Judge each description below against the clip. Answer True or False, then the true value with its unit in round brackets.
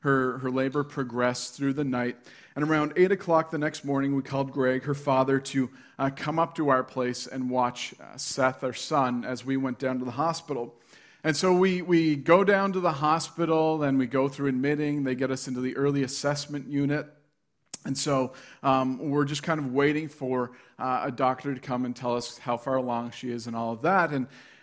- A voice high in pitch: False (135 Hz)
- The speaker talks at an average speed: False (215 wpm)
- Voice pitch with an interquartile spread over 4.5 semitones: False (2.6 semitones)